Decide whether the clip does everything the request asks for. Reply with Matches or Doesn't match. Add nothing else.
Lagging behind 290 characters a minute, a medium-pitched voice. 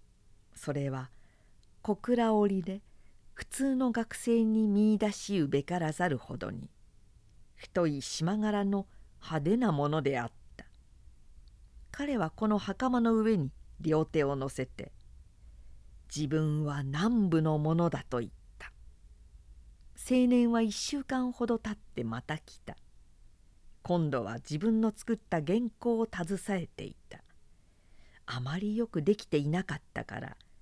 Matches